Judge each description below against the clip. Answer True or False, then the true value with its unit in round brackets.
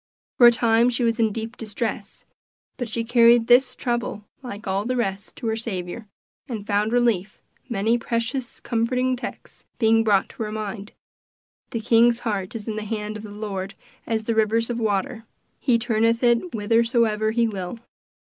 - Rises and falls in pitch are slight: True (1.9 semitones)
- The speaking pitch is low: False (225 Hz)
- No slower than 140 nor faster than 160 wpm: False (175 wpm)